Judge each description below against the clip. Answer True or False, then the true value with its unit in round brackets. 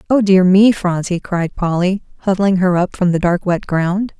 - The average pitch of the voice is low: False (185 Hz)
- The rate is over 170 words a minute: True (200 wpm)